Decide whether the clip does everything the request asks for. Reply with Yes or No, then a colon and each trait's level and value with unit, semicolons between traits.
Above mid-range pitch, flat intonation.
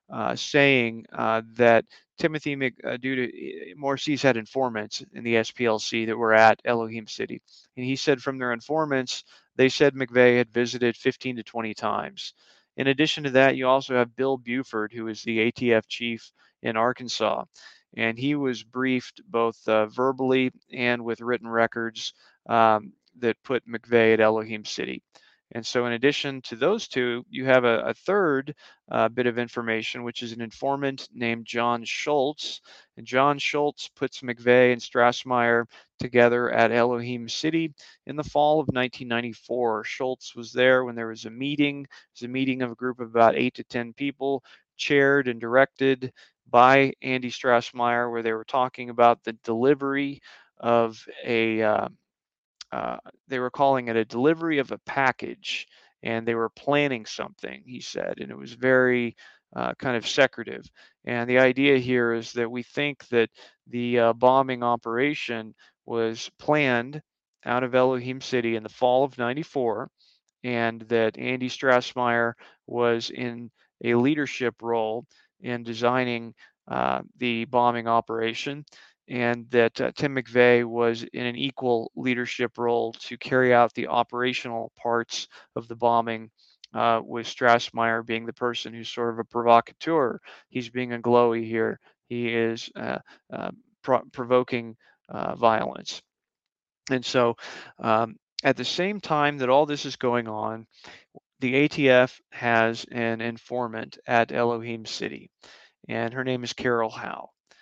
No: low, 120 Hz; narrow, 2.1 semitones